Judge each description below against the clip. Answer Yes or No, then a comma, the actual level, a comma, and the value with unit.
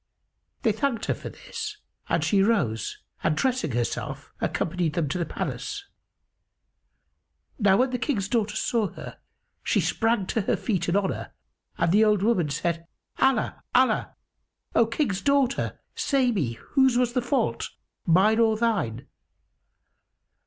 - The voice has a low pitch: No, high, 215 Hz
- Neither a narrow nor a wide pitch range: No, wide, 5.7 semitones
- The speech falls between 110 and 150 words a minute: Yes, average, 145 wpm